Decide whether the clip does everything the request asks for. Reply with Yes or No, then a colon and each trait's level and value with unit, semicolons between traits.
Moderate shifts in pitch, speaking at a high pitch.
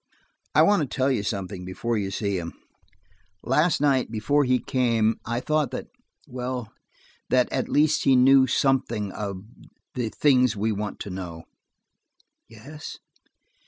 No: average, 4.4 semitones; low, 125 Hz